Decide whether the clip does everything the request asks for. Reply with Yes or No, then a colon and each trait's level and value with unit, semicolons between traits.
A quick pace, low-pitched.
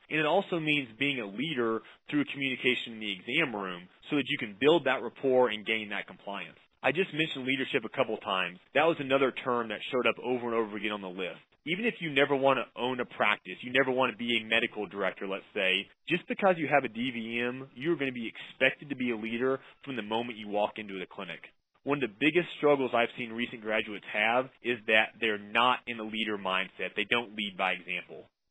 Yes: fast, 235 wpm; low, 120 Hz